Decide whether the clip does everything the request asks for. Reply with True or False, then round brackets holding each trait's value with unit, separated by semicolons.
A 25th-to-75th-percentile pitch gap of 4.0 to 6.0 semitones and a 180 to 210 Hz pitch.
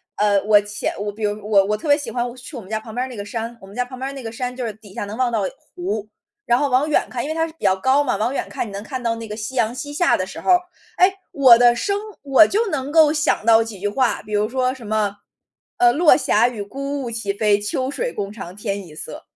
False (4.5 semitones; 235 Hz)